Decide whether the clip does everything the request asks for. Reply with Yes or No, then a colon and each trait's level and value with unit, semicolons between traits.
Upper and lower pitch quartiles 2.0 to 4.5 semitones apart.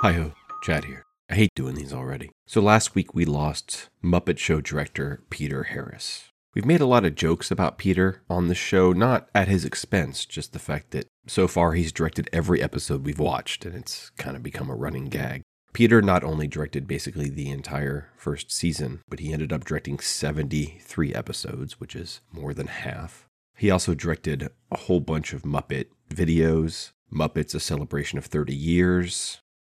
Yes: average, 3.7 semitones